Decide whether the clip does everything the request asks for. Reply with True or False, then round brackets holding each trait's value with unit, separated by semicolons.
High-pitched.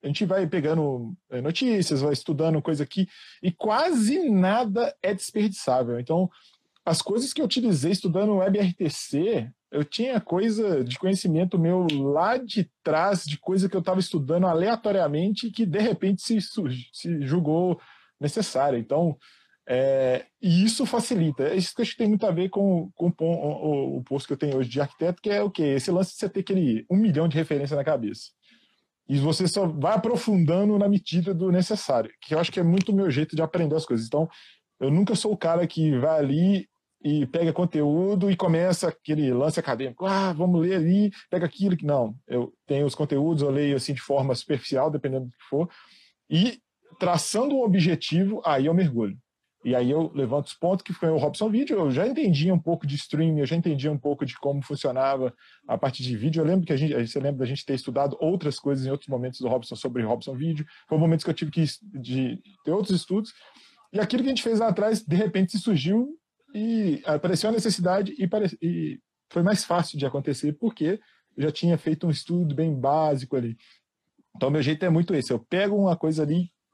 False (170 Hz)